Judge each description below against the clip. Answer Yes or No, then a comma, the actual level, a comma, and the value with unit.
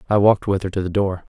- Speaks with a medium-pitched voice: No, very low, 95 Hz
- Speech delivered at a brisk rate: Yes, fast, 315 wpm